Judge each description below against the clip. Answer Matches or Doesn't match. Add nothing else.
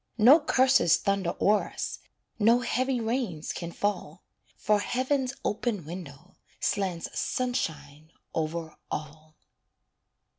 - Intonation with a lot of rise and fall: Matches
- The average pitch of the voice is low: Doesn't match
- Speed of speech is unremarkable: Doesn't match